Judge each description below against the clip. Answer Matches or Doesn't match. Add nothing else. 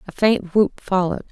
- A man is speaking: Doesn't match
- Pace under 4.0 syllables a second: Doesn't match